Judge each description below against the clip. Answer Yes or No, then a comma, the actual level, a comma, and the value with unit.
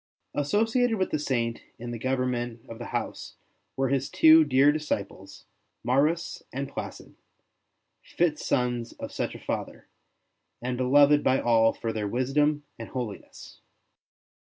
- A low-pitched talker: Yes, low, 130 Hz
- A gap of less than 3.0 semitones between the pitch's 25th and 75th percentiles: No, average, 3.6 semitones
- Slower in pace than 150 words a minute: Yes, slow, 135 wpm